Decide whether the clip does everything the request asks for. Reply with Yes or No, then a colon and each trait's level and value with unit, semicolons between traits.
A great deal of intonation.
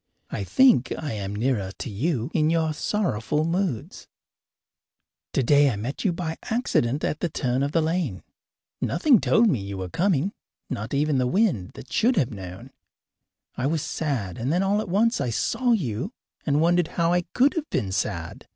Yes: wide, 7.3 semitones